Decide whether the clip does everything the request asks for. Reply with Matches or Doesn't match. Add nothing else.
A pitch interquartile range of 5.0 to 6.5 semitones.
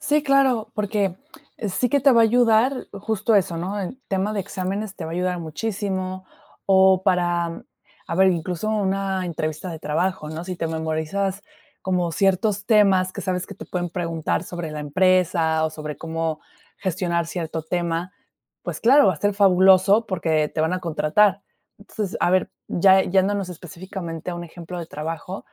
Doesn't match